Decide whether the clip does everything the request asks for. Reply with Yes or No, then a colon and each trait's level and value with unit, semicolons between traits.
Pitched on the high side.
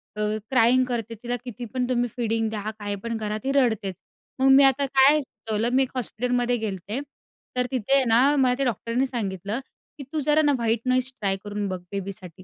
Yes: high, 240 Hz